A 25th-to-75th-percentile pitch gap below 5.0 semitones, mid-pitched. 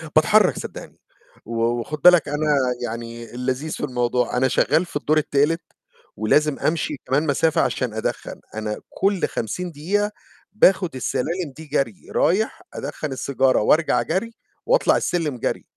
No: average, 5.3 semitones; medium, 150 Hz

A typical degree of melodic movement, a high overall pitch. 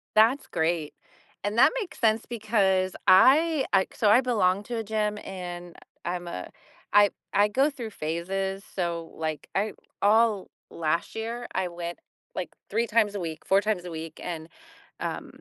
Yes: average, 4.2 semitones; high, 195 Hz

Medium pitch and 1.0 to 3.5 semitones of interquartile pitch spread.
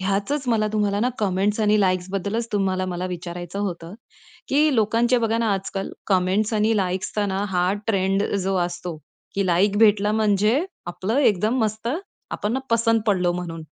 No: high, 200 Hz; average, 2.8 semitones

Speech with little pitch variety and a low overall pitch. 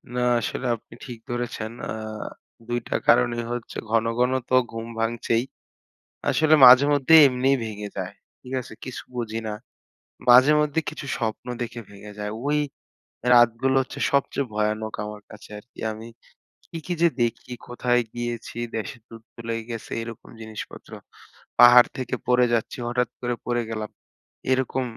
Yes: narrow, 2.1 semitones; low, 120 Hz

